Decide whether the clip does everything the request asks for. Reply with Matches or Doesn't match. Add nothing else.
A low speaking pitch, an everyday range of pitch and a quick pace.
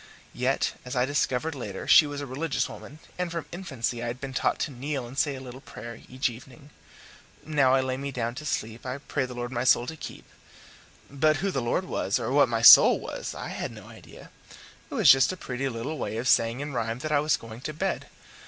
Matches